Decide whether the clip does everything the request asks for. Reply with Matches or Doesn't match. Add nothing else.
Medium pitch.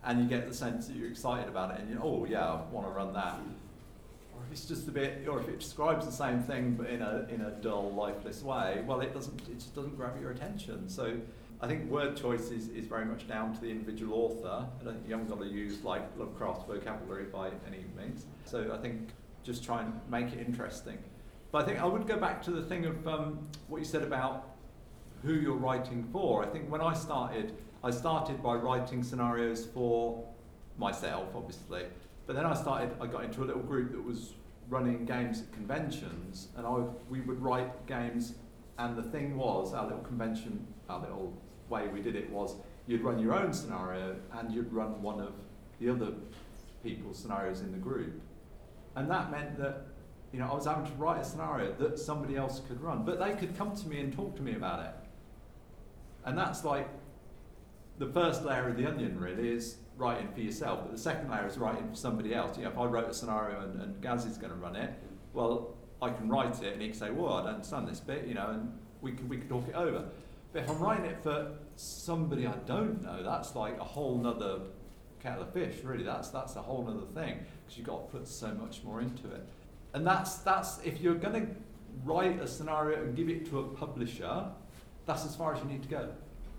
Doesn't match